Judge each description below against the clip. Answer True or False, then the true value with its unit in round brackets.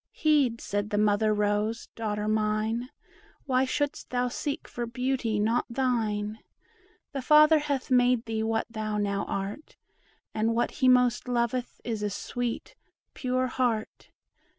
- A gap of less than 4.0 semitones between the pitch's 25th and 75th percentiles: True (3.0 semitones)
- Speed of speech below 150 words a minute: True (140 wpm)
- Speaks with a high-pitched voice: True (235 Hz)